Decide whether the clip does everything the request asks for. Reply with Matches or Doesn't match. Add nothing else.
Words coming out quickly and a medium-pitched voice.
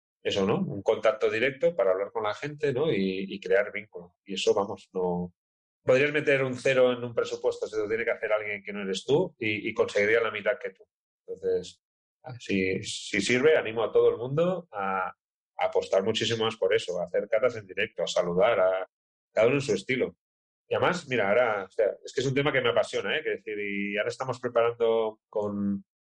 Matches